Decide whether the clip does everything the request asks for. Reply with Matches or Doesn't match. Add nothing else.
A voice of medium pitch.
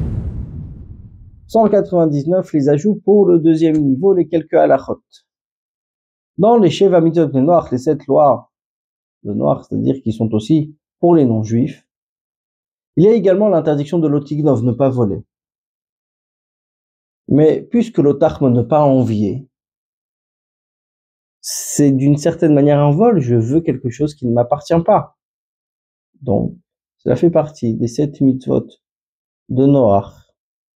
Matches